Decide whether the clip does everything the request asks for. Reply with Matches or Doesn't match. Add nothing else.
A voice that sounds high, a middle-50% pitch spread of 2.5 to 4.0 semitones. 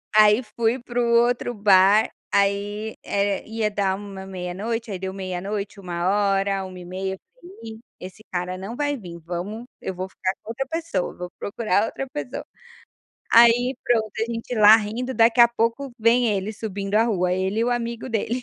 Matches